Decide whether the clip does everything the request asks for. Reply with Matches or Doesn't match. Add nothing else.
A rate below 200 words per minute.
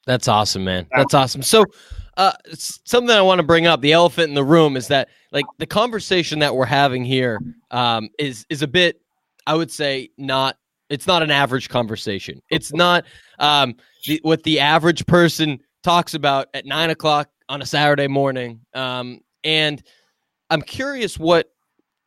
Matches